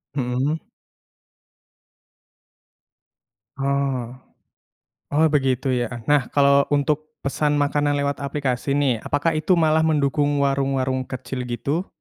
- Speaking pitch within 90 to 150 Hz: Yes, medium, 140 Hz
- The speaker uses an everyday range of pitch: No, narrow, 2.0 semitones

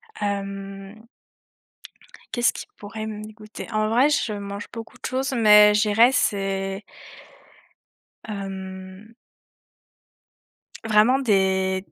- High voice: Yes, high, 210 Hz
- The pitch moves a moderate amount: No, narrow, 2.1 semitones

